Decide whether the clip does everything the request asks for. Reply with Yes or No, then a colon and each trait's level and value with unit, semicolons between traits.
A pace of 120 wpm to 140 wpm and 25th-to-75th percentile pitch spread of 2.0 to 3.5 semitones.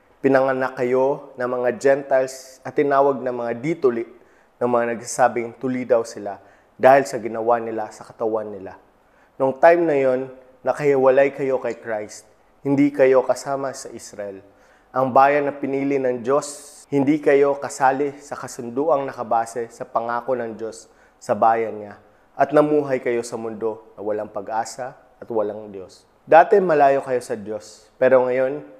No: average, 150 wpm; average, 3.0 semitones